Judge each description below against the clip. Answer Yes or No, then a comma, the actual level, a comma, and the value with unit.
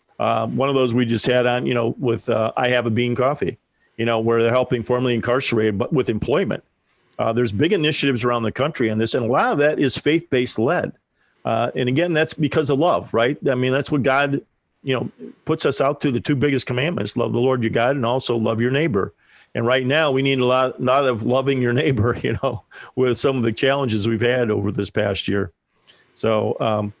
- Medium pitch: No, low, 125 Hz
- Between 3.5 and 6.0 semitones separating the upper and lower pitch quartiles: No, average, 2.9 semitones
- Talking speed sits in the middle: No, fast, 235 wpm